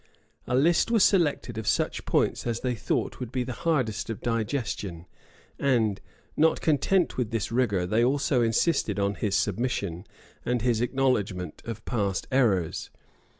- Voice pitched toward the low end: Yes, low, 120 Hz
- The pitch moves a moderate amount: Yes, average, 4.2 semitones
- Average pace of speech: Yes, average, 150 wpm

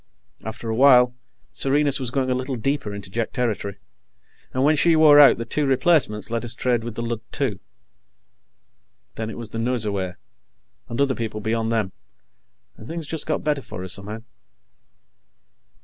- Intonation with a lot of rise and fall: No, average, 3.9 semitones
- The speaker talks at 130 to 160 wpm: No, average, 170 wpm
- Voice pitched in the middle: No, low, 120 Hz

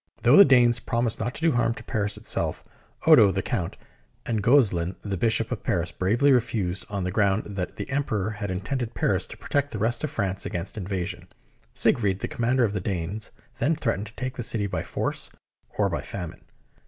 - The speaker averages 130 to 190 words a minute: No, average, 200 wpm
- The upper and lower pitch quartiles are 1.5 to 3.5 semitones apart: No, average, 4.0 semitones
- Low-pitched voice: Yes, low, 110 Hz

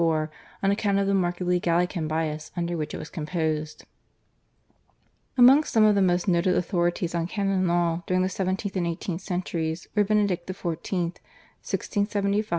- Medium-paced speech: Yes, average, 155 wpm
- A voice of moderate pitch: Yes, medium, 180 Hz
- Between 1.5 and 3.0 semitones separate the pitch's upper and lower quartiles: Yes, average, 2.7 semitones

